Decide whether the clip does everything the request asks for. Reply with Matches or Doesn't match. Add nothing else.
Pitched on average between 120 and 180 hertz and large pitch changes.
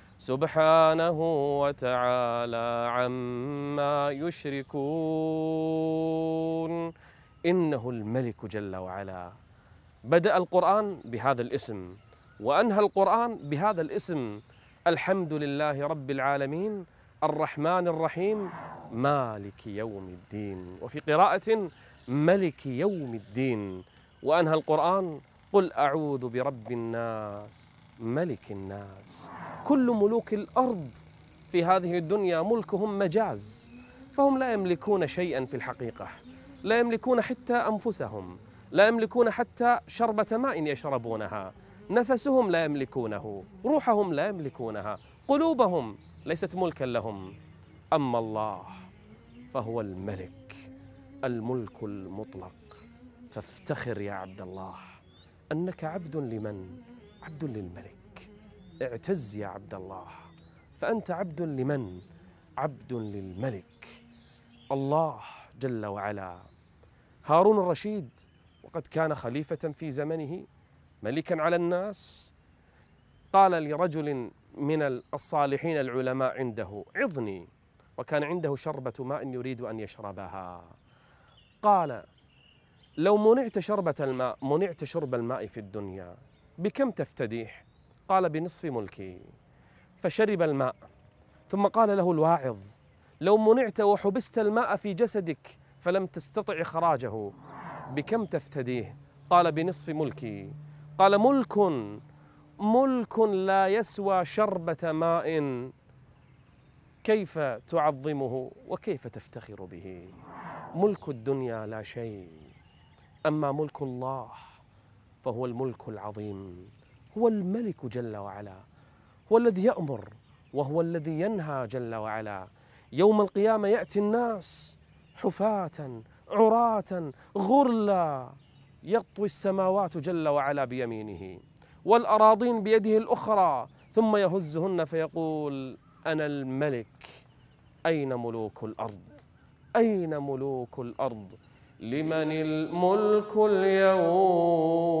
Matches